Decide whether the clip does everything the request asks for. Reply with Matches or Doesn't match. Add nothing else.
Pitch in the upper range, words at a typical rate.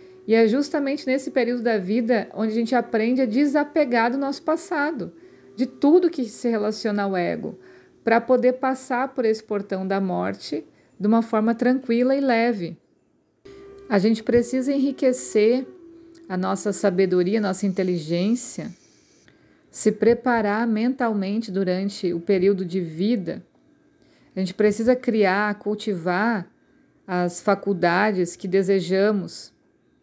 Matches